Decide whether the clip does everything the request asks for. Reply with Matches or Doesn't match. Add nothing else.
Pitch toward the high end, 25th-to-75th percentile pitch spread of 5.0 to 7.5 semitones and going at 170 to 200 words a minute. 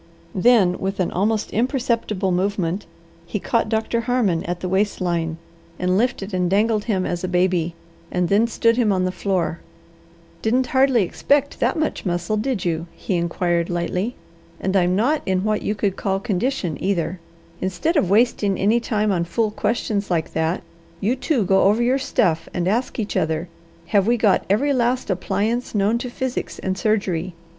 Doesn't match